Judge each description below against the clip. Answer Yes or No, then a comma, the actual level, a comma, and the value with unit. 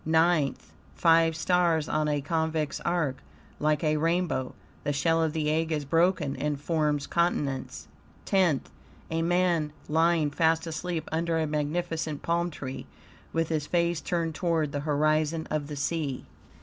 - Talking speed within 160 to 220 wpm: No, average, 150 wpm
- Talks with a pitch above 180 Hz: No, medium, 160 Hz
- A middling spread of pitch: No, narrow, 2.0 semitones